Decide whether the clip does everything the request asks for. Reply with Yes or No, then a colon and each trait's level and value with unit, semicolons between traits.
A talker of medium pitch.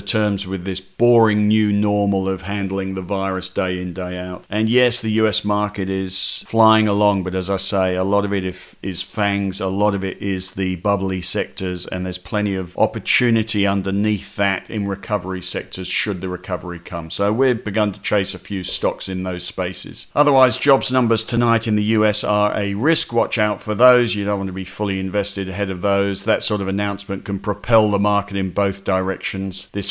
No: low, 100 Hz